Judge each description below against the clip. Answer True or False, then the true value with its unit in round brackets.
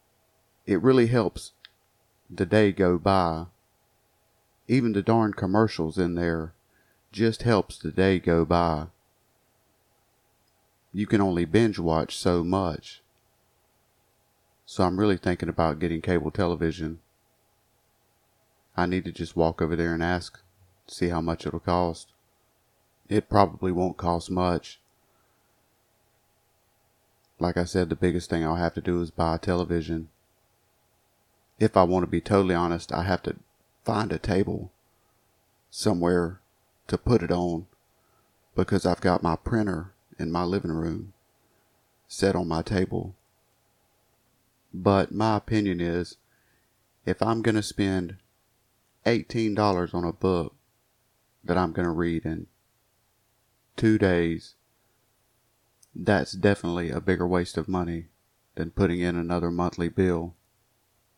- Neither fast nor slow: False (130 wpm)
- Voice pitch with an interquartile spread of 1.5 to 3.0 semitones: False (4.2 semitones)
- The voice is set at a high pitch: False (95 Hz)